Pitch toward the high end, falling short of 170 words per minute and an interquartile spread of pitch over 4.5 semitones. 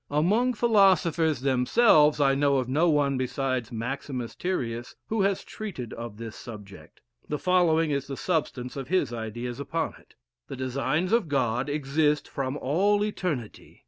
No: medium, 140 Hz; average, 150 wpm; average, 5.3 semitones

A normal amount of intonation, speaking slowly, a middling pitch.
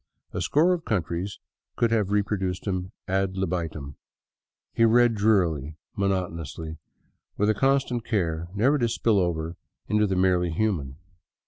No: average, 4.5 semitones; slow, 130 wpm; very low, 95 Hz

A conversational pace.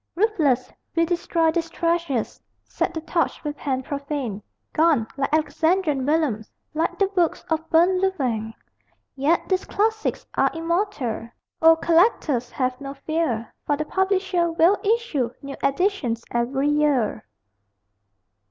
No: slow, 130 wpm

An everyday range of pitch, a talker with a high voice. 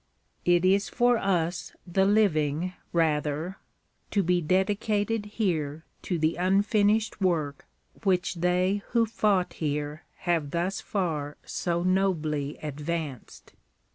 No: average, 4.1 semitones; medium, 180 Hz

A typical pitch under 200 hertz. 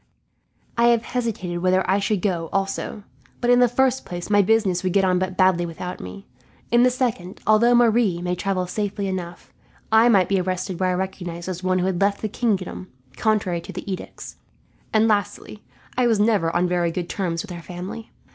Yes: high, 190 Hz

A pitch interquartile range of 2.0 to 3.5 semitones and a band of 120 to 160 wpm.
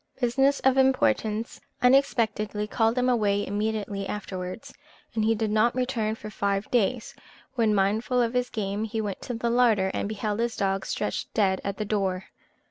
No: average, 2.9 semitones; average, 170 wpm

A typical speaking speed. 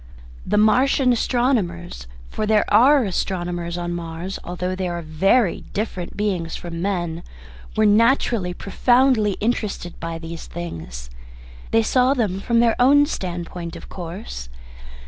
No: slow, 130 wpm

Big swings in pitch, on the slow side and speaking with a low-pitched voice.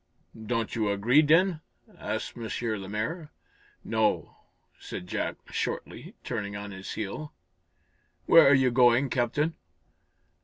Yes: wide, 5.9 semitones; slow, 115 wpm; low, 120 Hz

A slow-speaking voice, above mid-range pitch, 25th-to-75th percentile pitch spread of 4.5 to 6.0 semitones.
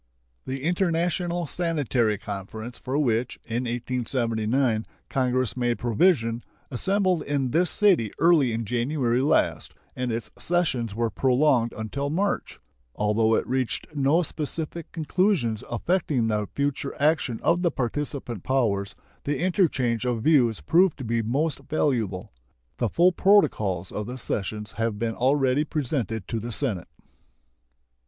No: slow, 130 wpm; low, 125 Hz; wide, 5.4 semitones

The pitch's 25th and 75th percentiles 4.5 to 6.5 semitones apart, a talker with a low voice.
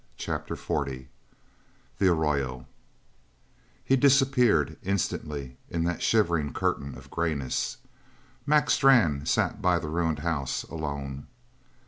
Yes: average, 4.9 semitones; very low, 80 Hz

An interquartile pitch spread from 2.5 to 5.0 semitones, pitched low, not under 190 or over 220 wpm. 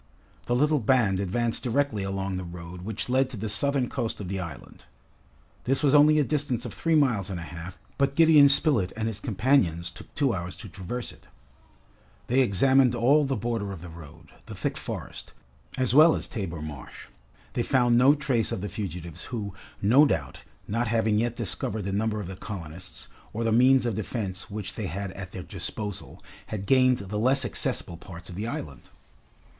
No: wide, 5.5 semitones; low, 110 Hz; average, 195 wpm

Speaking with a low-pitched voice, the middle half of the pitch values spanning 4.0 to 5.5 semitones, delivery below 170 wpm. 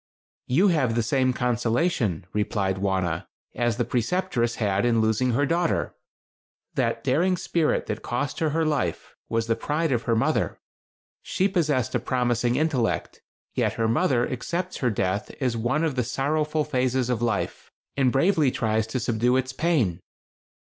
Yes: low, 125 Hz; average, 4.9 semitones; average, 160 wpm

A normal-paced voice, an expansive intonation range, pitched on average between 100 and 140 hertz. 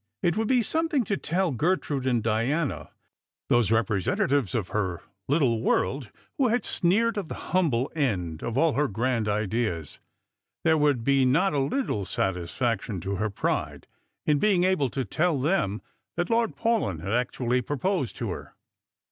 Yes: average, 160 wpm; wide, 7.9 semitones; low, 135 Hz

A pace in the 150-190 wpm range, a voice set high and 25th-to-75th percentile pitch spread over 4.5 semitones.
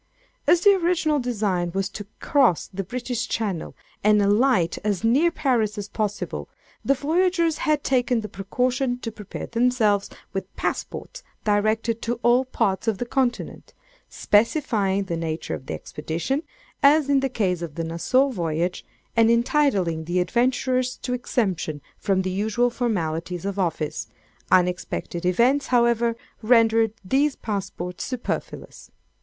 No: average, 140 wpm; high, 225 Hz; average, 5.2 semitones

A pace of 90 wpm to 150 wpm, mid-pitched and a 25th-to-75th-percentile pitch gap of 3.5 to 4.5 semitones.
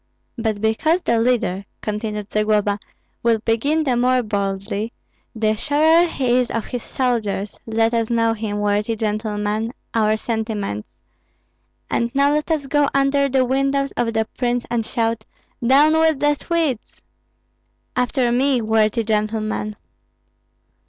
No: slow, 135 wpm; high, 230 Hz; average, 3.9 semitones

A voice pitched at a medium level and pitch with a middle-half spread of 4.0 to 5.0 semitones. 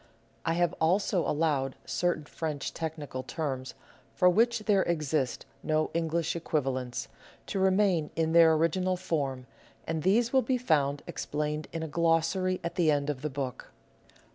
No: medium, 160 Hz; average, 3.5 semitones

